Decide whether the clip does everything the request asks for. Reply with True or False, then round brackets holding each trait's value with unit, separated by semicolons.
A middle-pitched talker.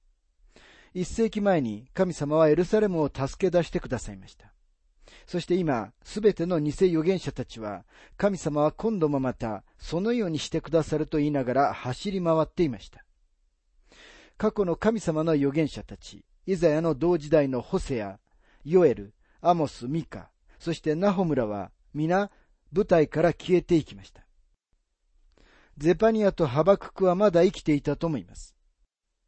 True (155 Hz)